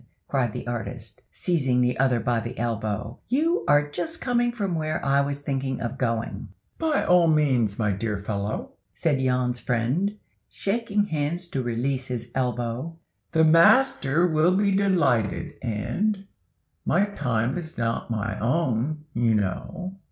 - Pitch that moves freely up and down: Yes, wide, 6.7 semitones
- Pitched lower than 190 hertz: Yes, low, 135 Hz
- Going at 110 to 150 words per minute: Yes, average, 145 wpm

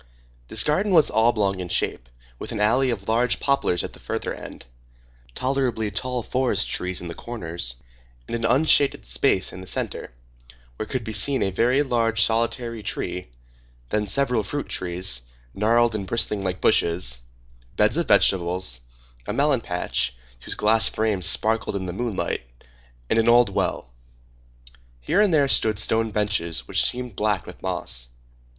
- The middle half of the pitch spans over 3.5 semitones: Yes, average, 4.7 semitones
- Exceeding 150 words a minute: Yes, average, 160 wpm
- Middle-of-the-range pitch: No, low, 110 Hz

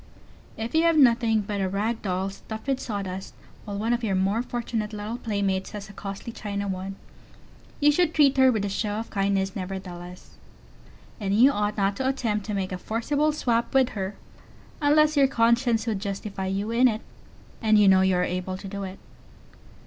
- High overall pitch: Yes, high, 210 Hz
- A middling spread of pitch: Yes, average, 3.3 semitones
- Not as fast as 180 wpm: No, average, 195 wpm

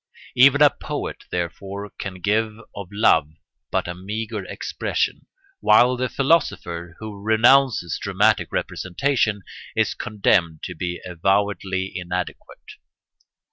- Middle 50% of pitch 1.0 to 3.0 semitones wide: No, average, 4.0 semitones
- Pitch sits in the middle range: No, low, 100 Hz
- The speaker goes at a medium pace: No, slow, 110 wpm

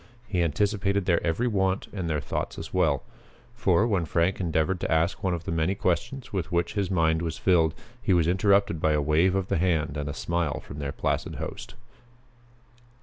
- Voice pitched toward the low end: Yes, very low, 85 Hz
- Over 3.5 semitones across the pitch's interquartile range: No, average, 3.1 semitones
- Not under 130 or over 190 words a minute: No, average, 200 wpm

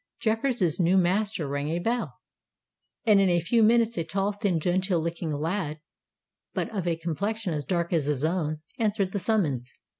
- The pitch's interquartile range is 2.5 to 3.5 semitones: No, average, 4.4 semitones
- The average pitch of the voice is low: No, medium, 180 Hz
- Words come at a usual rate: Yes, average, 175 wpm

